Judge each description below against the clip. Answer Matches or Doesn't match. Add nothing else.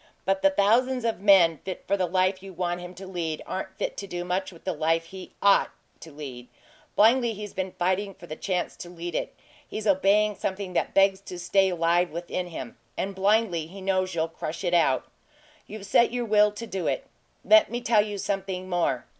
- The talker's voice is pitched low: Doesn't match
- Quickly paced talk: Matches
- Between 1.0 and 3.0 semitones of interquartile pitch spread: Matches